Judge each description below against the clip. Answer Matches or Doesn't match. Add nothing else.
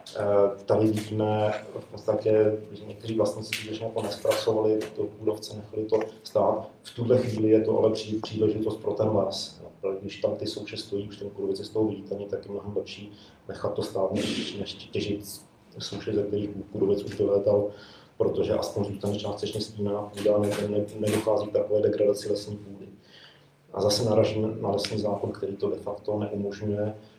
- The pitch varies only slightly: Matches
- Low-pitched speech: Matches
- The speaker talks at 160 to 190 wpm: Matches